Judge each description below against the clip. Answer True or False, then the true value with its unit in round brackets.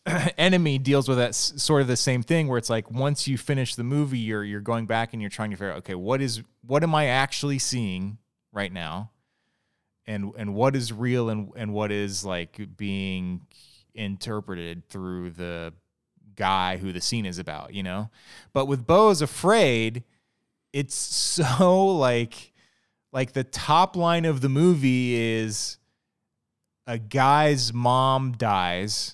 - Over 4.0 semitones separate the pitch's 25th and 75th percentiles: True (5.1 semitones)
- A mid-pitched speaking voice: False (115 Hz)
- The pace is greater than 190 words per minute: False (160 wpm)